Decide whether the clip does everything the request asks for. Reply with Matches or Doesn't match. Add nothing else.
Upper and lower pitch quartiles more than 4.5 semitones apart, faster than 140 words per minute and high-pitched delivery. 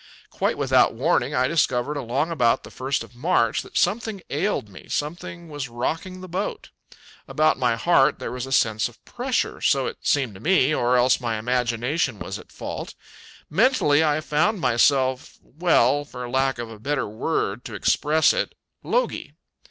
Doesn't match